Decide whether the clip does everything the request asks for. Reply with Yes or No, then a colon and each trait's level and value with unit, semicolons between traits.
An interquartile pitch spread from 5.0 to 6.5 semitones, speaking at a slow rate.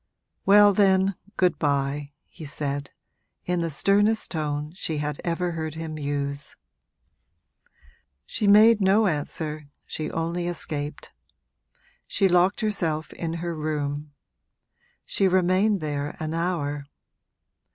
No: average, 4.2 semitones; slow, 115 wpm